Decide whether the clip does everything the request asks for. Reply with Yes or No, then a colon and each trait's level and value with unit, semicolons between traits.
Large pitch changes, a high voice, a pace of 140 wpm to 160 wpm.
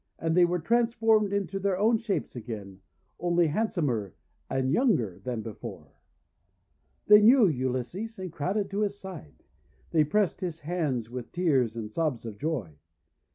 No: wide, 8.5 semitones; medium, 165 Hz; average, 150 wpm